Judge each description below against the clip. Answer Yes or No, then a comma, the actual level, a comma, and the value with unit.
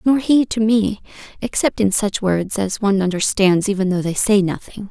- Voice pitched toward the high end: Yes, high, 205 Hz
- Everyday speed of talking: Yes, average, 185 wpm